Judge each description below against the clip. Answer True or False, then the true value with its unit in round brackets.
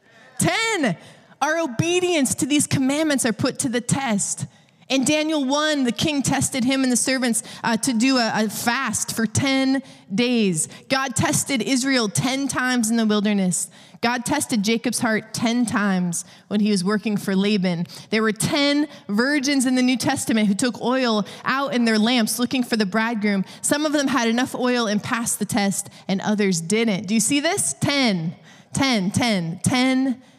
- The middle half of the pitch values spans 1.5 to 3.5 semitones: False (4.4 semitones)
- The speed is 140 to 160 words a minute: False (180 wpm)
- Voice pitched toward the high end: True (230 Hz)